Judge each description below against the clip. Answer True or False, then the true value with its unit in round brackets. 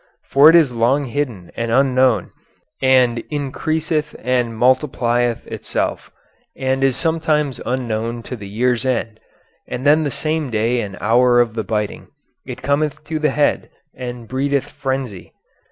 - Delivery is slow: False (145 wpm)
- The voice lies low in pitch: True (130 Hz)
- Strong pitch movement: False (3.4 semitones)